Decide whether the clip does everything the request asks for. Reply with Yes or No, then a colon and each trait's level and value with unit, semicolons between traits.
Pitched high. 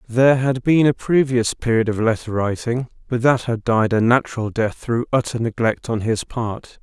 No: low, 120 Hz